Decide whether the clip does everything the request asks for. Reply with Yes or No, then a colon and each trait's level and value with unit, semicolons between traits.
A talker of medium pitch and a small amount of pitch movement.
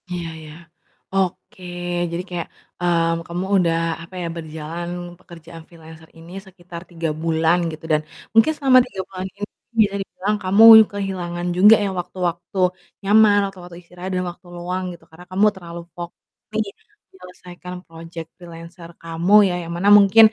Yes: medium, 175 Hz; narrow, 2.2 semitones